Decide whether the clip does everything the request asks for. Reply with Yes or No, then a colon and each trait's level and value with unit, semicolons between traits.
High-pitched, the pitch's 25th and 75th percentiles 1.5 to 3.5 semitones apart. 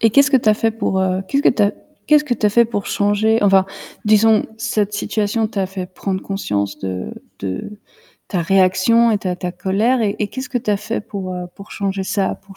Yes: high, 205 Hz; average, 2.9 semitones